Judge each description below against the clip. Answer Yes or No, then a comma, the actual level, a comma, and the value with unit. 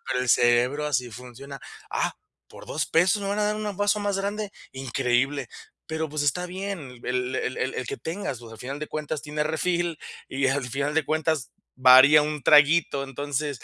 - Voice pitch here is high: No, medium, 145 Hz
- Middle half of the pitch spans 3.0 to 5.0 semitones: Yes, average, 4.2 semitones